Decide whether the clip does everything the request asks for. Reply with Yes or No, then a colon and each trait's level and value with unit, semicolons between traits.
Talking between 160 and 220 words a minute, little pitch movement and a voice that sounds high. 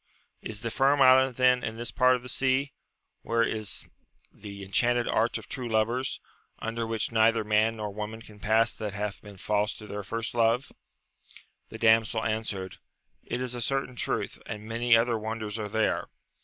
No: average, 185 wpm; narrow, 2.2 semitones; low, 115 Hz